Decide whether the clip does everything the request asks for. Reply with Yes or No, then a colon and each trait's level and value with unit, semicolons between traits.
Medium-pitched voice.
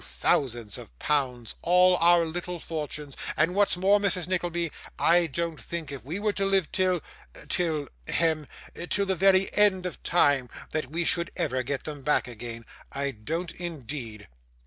Yes: medium, 165 Hz